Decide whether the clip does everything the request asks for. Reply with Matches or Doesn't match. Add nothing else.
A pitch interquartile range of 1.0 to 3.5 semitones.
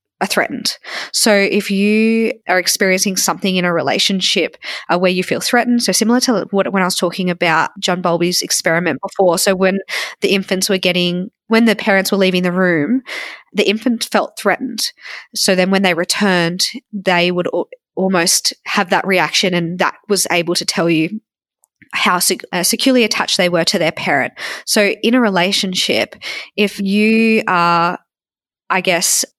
Matches